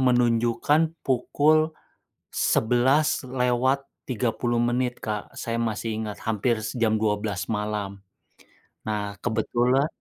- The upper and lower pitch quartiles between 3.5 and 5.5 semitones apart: No, average, 2.9 semitones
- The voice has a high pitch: No, low, 120 Hz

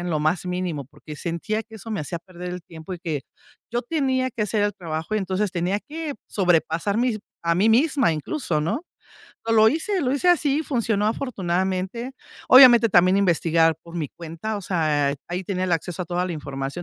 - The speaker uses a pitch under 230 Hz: Yes, medium, 185 Hz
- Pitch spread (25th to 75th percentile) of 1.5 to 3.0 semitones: No, average, 5.3 semitones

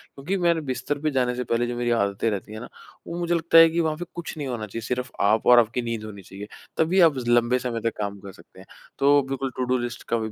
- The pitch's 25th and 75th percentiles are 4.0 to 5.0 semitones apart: Yes, average, 4.6 semitones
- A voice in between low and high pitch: No, low, 125 Hz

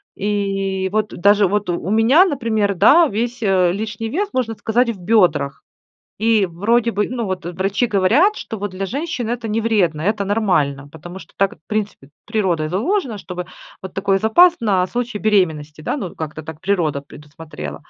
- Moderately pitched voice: No, high, 200 Hz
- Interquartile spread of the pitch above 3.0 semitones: Yes, average, 4.0 semitones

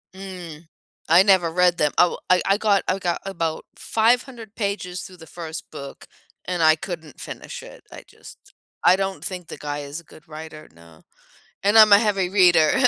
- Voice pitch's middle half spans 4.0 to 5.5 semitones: No, average, 3.6 semitones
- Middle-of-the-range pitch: Yes, medium, 180 Hz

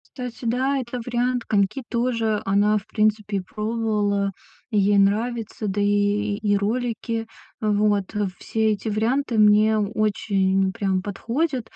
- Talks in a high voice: Yes, high, 215 Hz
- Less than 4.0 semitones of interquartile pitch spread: Yes, narrow, 2.4 semitones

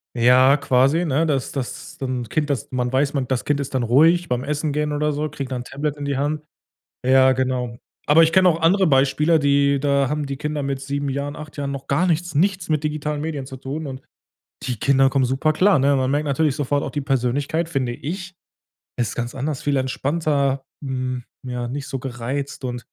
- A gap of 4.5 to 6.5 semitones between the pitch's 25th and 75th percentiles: No, narrow, 2.4 semitones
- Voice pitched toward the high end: No, medium, 140 Hz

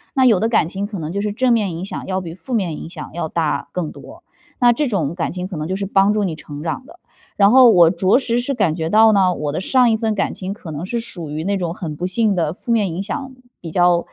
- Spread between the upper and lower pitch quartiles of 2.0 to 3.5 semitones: No, average, 4.7 semitones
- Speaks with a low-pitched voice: No, high, 190 Hz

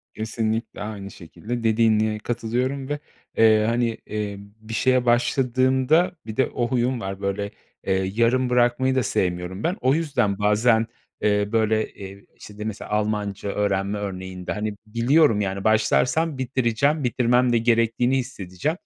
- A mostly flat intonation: No, average, 3.4 semitones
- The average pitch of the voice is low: Yes, low, 115 Hz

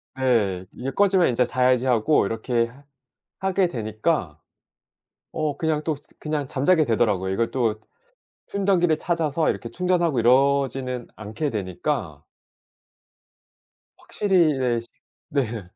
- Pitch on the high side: No, low, 130 Hz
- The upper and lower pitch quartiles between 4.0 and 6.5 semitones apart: Yes, wide, 5.4 semitones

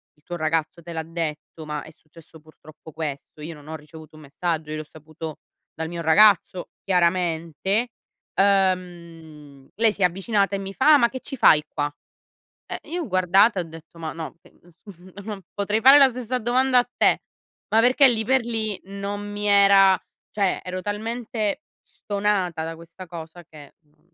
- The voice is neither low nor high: Yes, medium, 180 Hz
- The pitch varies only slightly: No, average, 4.6 semitones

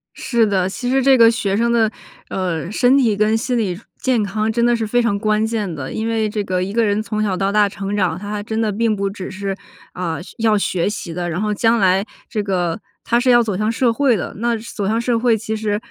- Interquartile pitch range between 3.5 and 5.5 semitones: No, average, 2.8 semitones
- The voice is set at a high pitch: Yes, high, 215 Hz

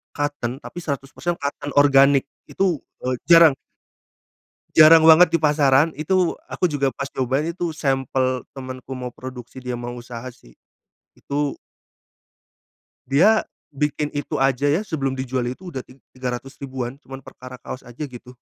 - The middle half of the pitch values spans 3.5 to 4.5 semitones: No, average, 2.9 semitones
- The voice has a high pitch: No, low, 135 Hz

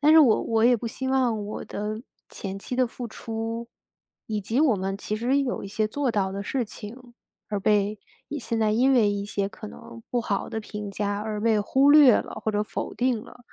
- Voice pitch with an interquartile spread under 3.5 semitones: Yes, average, 3.0 semitones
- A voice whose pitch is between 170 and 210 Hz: No, high, 220 Hz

